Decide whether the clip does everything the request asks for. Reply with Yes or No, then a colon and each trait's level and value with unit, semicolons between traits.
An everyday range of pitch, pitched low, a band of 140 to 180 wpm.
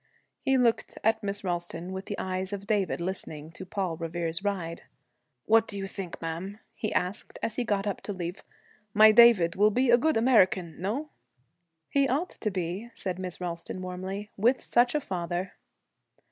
No: average, 3.7 semitones; high, 195 Hz; average, 175 wpm